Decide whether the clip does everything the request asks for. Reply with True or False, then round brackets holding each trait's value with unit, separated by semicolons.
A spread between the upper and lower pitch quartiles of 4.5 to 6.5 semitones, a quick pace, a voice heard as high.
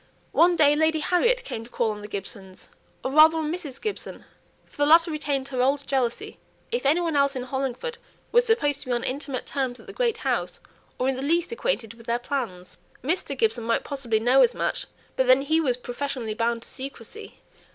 True (4.8 semitones; 210 wpm; 275 Hz)